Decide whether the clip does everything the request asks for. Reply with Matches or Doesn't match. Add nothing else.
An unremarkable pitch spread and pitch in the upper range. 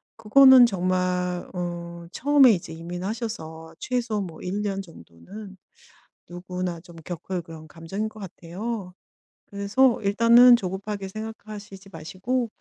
Matches